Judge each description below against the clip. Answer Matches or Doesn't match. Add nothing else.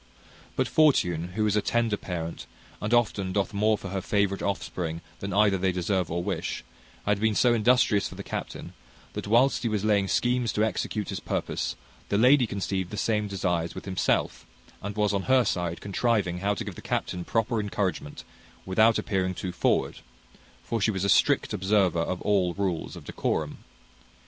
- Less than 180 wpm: Doesn't match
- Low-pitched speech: Matches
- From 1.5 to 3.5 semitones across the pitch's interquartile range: Matches